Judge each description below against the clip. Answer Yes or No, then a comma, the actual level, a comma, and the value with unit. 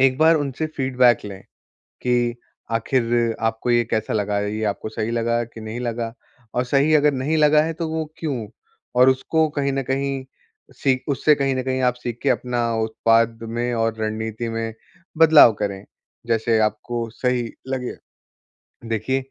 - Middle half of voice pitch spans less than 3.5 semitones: Yes, average, 3.0 semitones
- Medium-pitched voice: No, low, 120 Hz